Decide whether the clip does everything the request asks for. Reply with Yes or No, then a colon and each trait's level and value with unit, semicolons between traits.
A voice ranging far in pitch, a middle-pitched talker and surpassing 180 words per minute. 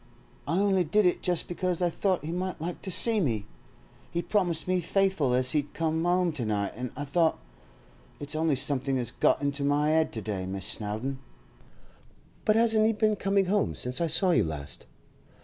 Yes: wide, 6.2 semitones; medium, 160 Hz; average, 190 wpm